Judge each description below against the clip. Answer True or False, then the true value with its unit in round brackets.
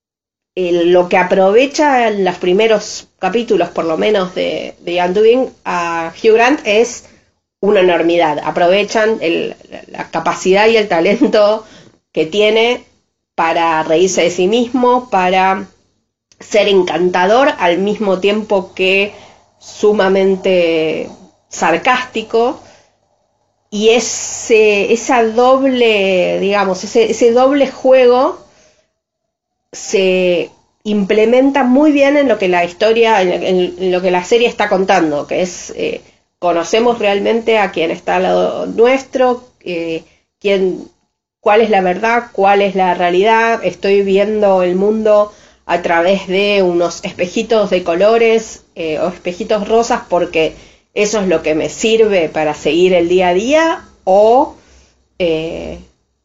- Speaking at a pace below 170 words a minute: True (125 wpm)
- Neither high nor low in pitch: False (200 Hz)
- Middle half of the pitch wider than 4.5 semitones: False (4.1 semitones)